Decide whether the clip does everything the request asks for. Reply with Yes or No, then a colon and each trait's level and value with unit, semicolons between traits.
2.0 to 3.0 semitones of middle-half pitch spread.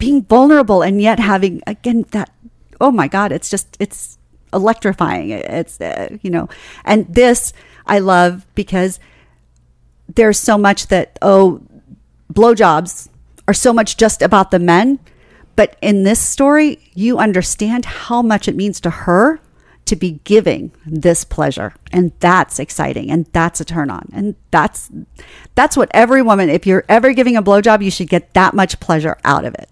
No: average, 4.1 semitones